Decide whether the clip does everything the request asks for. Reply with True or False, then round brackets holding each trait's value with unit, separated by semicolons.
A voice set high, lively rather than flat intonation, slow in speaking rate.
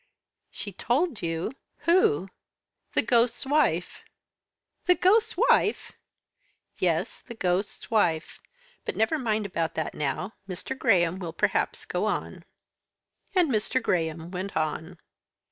True (200 Hz; 7.4 semitones; 120 wpm)